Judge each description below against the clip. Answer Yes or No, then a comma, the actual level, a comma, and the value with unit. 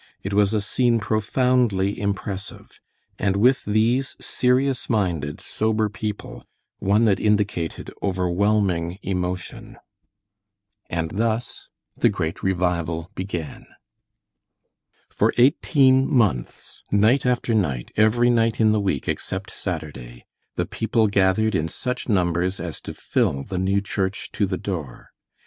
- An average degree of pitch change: Yes, average, 3.8 semitones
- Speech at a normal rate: No, slow, 125 wpm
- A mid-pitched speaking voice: No, low, 100 Hz